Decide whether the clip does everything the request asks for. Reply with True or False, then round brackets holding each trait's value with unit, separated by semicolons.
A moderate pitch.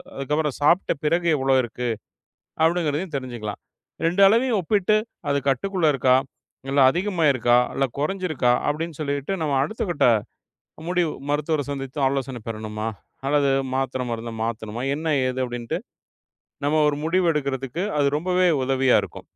True (145 Hz)